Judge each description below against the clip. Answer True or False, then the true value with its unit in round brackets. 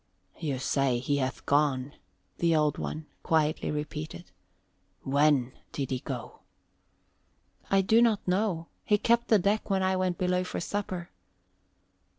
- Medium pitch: True (160 Hz)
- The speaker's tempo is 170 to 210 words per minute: False (140 wpm)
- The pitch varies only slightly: False (5.0 semitones)